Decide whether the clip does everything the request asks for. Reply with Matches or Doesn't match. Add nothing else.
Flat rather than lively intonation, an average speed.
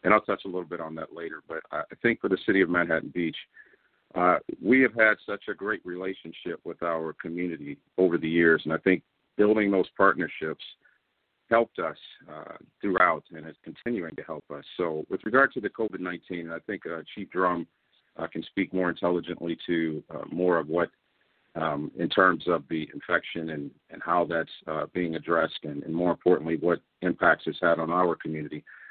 Matches